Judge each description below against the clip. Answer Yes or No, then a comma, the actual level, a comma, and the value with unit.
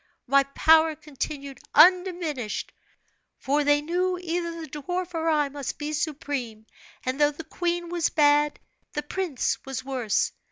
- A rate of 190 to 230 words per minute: No, average, 145 wpm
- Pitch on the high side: Yes, very high, 300 Hz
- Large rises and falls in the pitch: No, average, 3.4 semitones